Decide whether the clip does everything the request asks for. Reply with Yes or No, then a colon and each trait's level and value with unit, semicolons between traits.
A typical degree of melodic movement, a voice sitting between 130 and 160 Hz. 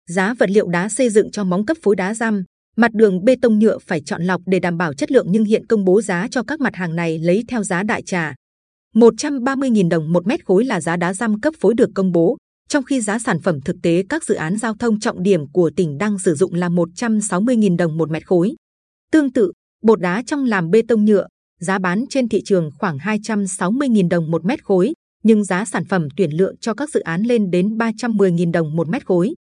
No: average, 4.4 semitones; high, 200 Hz